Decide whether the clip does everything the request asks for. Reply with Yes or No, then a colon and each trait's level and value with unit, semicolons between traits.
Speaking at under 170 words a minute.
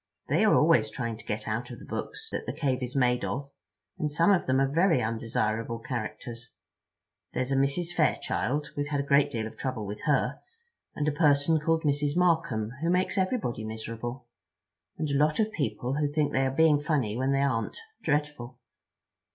No: average, 185 wpm